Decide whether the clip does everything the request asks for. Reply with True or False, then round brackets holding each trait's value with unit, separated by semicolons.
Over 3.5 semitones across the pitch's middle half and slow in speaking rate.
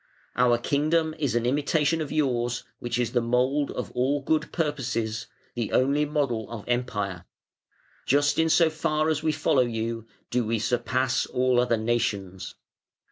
False (4.0 semitones; 155 wpm)